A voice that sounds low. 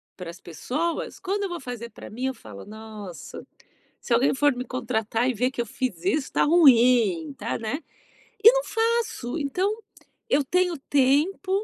No: very high, 255 Hz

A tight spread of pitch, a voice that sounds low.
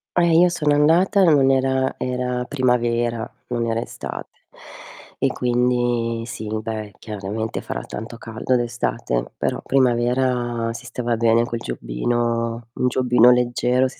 Yes: narrow, 1.7 semitones; low, 120 Hz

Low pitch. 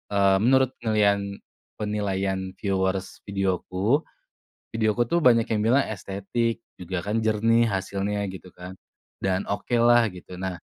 Yes: low, 100 Hz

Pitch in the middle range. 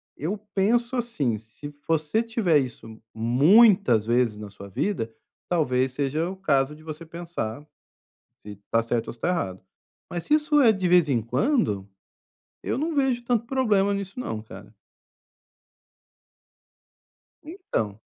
Yes: medium, 155 Hz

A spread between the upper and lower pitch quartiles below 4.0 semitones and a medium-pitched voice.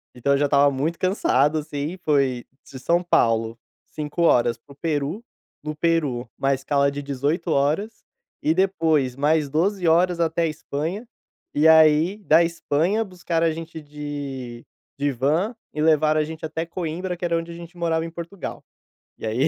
Yes: average, 3.1 semitones; medium, 155 Hz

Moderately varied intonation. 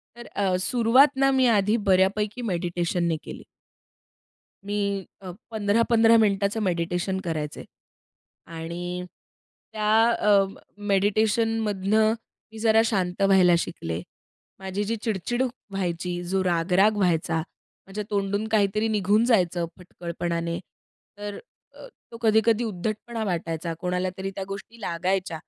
Yes: average, 3.5 semitones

